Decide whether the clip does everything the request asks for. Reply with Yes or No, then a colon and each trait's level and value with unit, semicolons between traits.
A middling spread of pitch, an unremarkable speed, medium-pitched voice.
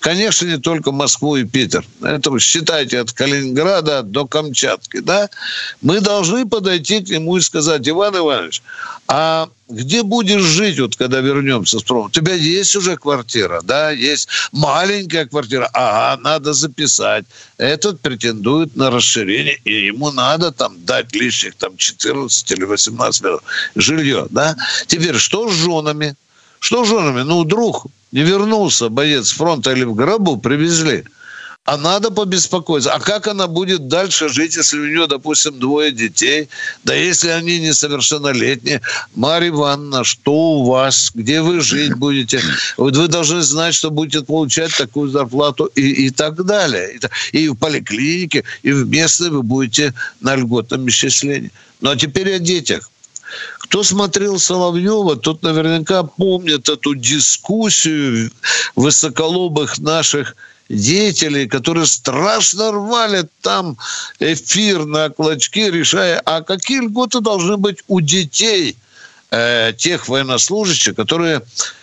Yes: average, 4.7 semitones; average, 140 wpm; medium, 155 Hz